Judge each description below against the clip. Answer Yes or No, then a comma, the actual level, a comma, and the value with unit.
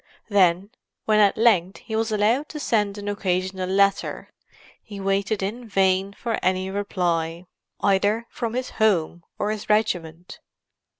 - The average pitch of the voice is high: Yes, high, 200 Hz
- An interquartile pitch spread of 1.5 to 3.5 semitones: Yes, narrow, 2.6 semitones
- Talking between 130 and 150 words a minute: Yes, average, 140 wpm